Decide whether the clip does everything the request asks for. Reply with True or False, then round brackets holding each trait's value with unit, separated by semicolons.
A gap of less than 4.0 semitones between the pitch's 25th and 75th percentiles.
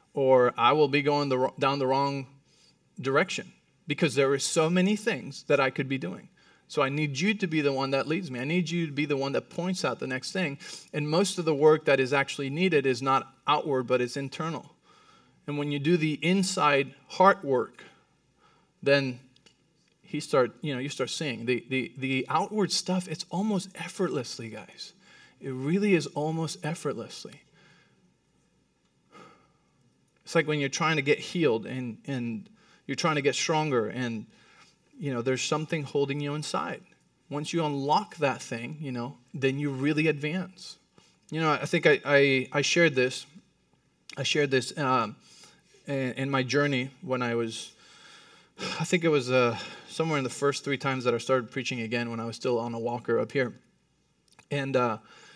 True (3.4 semitones)